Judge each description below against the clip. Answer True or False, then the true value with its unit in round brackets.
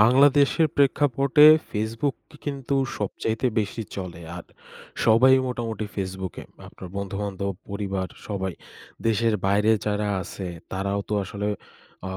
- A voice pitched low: True (105 Hz)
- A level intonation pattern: False (4.4 semitones)